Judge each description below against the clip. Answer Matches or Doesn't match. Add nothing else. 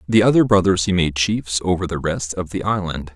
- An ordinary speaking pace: Doesn't match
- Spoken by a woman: Doesn't match